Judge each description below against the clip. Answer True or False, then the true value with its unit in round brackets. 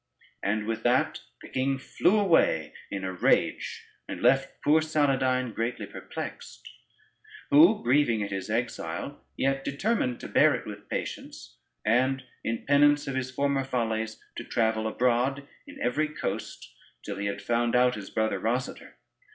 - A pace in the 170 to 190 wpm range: False (150 wpm)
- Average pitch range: True (3.8 semitones)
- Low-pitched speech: True (125 Hz)